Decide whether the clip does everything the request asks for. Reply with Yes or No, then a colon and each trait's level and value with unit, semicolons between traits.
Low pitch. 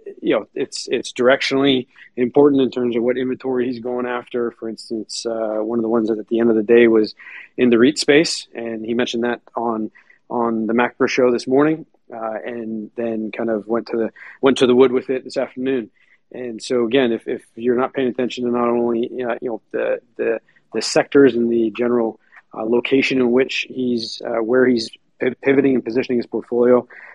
Yes: low, 120 Hz